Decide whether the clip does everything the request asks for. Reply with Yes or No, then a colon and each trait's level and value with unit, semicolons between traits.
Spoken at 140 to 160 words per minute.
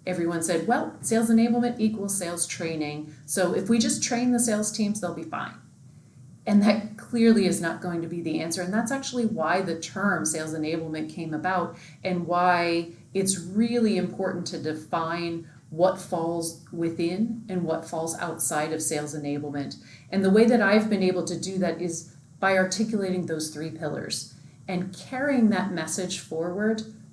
No: average, 170 wpm